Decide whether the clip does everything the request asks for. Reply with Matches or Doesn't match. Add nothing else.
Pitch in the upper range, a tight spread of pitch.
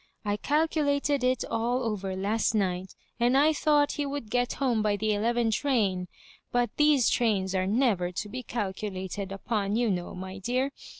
Doesn't match